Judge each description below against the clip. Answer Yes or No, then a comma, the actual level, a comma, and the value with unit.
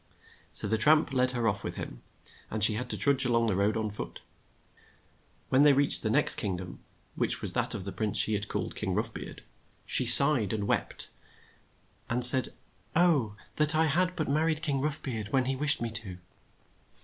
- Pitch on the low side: Yes, low, 125 Hz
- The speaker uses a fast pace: Yes, fast, 210 wpm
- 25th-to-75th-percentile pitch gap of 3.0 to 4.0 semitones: No, average, 5.0 semitones